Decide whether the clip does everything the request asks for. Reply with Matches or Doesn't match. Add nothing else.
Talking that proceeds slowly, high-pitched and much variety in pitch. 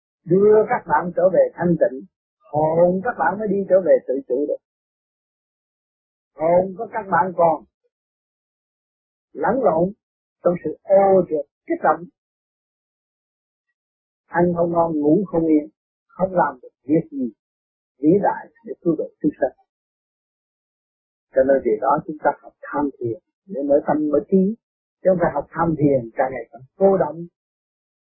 Doesn't match